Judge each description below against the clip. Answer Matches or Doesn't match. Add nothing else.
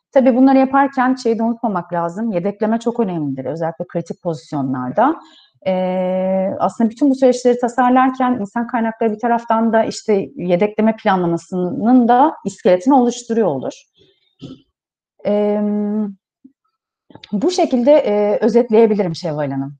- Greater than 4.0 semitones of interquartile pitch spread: Matches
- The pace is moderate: Matches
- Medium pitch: Doesn't match